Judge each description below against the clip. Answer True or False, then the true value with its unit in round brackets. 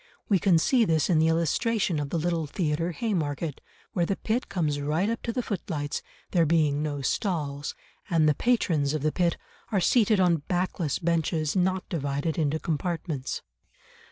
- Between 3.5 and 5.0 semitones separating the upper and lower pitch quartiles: True (3.8 semitones)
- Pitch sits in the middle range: True (165 Hz)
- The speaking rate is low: False (170 wpm)